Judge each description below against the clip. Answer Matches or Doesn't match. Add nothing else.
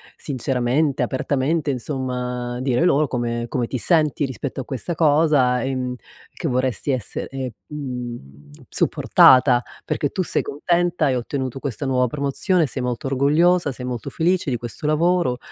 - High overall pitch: Doesn't match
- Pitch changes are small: Doesn't match